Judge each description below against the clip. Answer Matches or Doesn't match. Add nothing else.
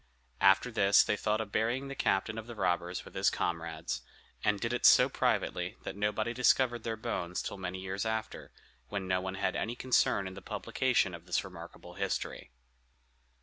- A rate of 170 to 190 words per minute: Matches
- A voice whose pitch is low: Matches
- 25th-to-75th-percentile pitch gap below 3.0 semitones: Doesn't match